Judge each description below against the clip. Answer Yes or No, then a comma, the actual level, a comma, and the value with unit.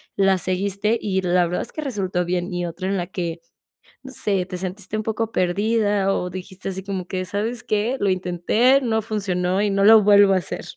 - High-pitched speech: Yes, high, 195 Hz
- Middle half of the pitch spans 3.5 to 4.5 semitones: No, narrow, 2.6 semitones